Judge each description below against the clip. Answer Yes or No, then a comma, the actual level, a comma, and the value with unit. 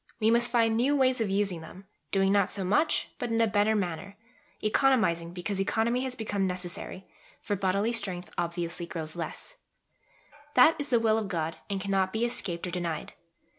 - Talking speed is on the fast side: No, average, 180 wpm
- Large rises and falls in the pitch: No, average, 4.2 semitones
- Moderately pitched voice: No, high, 200 Hz